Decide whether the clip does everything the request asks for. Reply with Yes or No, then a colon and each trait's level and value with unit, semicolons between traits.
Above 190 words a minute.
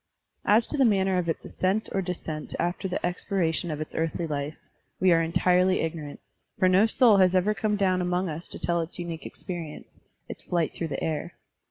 Yes: average, 200 wpm